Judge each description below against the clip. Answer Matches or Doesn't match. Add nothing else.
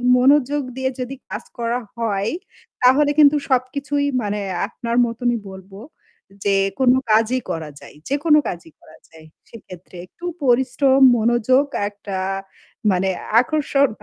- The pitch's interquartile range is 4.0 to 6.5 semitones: Matches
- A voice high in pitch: Matches